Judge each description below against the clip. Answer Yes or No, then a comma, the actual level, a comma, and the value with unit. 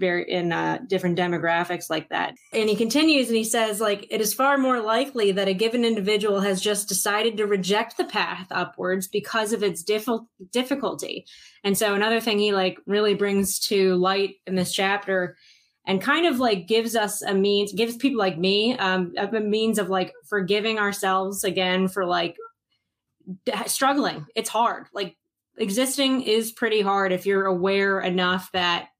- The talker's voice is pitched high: Yes, high, 205 Hz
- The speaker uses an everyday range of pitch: Yes, average, 3.0 semitones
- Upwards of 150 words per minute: Yes, average, 175 wpm